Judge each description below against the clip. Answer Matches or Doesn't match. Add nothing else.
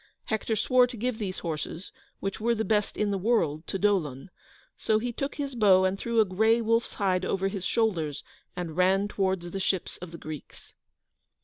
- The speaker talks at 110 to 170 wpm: Doesn't match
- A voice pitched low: Doesn't match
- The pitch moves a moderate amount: Matches